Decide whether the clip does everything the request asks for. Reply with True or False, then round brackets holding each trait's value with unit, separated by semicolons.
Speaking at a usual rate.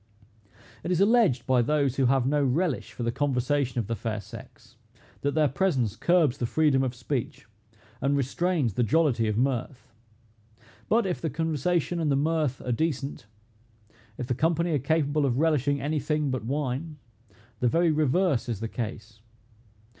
True (170 wpm)